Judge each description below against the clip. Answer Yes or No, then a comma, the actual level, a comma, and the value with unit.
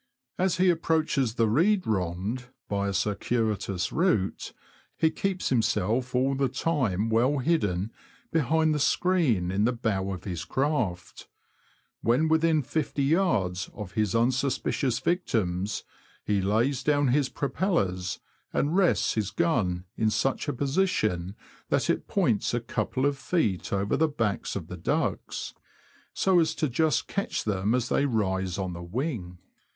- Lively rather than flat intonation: Yes, wide, 7.5 semitones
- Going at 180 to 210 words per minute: No, average, 145 wpm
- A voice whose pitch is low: Yes, low, 120 Hz